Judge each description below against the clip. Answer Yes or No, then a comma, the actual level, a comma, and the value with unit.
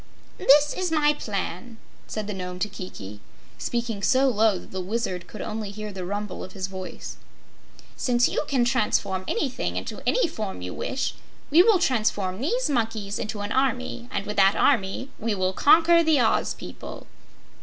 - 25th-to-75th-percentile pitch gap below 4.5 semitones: No, wide, 5.4 semitones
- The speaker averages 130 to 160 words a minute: No, average, 175 wpm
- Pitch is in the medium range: No, high, 220 Hz